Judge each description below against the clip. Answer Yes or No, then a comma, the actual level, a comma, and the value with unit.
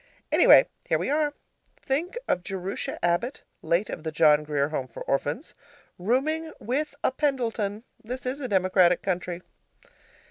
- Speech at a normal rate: Yes, average, 145 wpm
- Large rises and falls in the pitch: Yes, wide, 7.6 semitones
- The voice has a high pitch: Yes, high, 205 Hz